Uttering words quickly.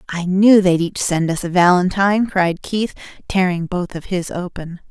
No: average, 185 wpm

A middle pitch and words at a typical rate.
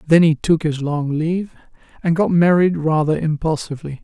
Yes: medium, 160 Hz; average, 165 wpm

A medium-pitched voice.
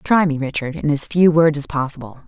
Yes: medium, 150 Hz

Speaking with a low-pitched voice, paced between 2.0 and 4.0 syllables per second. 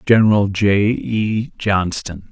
Yes: low, 105 Hz; 3.3 syllables/s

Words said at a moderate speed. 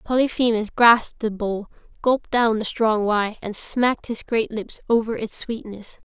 Yes: average, 165 wpm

